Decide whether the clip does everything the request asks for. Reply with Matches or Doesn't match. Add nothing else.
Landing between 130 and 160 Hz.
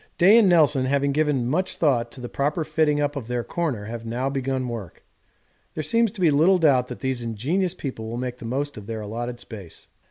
Matches